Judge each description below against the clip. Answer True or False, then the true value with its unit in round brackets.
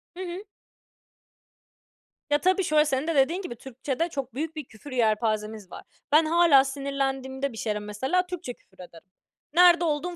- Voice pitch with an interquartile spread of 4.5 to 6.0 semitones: True (5.5 semitones)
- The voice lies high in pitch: True (275 Hz)